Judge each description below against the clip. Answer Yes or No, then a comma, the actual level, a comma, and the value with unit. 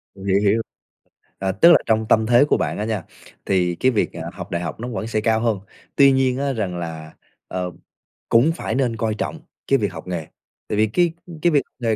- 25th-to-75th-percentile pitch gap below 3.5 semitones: No, average, 4.9 semitones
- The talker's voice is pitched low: Yes, low, 110 Hz